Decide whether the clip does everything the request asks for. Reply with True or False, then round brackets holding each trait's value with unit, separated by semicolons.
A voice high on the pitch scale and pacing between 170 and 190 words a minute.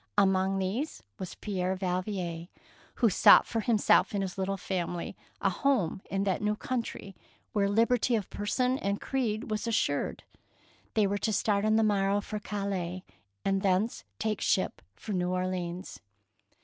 False (200 Hz; 160 wpm)